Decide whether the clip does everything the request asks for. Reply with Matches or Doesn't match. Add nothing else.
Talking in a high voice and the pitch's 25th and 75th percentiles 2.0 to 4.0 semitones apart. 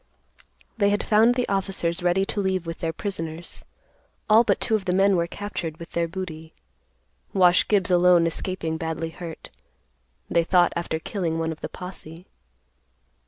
Doesn't match